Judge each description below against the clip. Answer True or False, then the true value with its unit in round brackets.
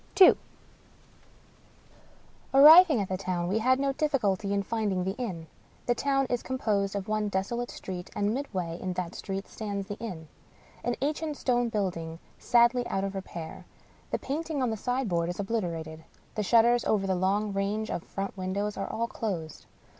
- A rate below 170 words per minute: False (175 wpm)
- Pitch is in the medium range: False (205 Hz)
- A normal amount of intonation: True (4.4 semitones)